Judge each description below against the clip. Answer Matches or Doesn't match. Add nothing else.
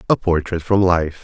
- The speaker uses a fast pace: Doesn't match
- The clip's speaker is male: Matches